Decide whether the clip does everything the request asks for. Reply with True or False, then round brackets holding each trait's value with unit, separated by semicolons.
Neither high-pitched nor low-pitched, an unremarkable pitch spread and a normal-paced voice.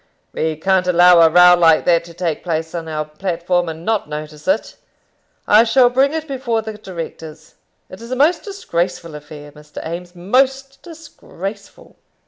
False (180 Hz; 5.9 semitones; 160 wpm)